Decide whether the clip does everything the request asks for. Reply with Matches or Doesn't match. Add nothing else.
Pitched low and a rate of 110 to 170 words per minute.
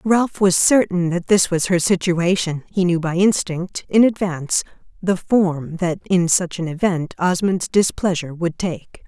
Doesn't match